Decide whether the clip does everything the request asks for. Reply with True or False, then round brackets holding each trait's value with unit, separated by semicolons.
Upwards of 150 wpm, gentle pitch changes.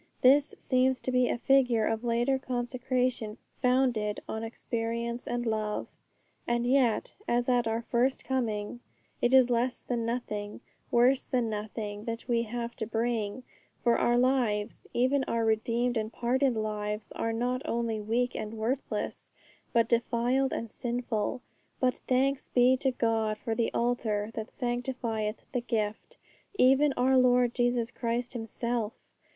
False (145 wpm; 2.0 semitones)